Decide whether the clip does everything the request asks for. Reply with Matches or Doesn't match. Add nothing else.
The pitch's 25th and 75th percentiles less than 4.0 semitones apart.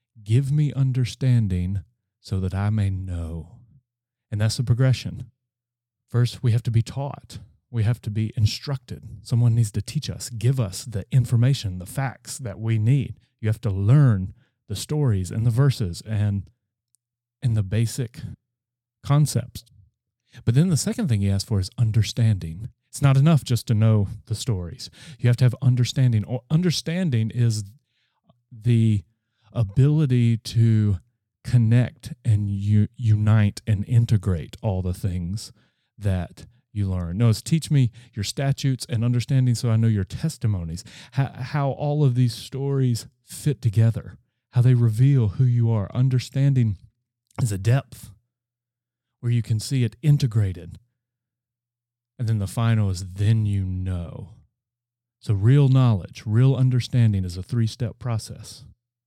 Matches